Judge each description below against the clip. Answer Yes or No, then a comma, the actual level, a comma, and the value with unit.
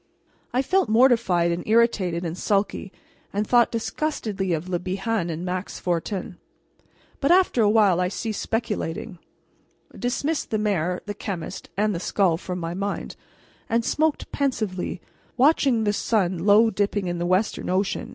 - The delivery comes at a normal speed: Yes, average, 150 wpm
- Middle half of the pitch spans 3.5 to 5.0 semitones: Yes, average, 4.2 semitones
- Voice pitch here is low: No, high, 205 Hz